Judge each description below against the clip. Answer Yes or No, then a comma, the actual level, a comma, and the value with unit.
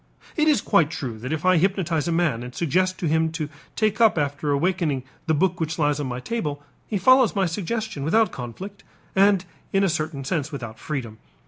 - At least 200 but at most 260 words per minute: Yes, fast, 205 wpm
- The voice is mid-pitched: Yes, medium, 160 Hz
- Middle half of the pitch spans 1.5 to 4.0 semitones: No, average, 5.1 semitones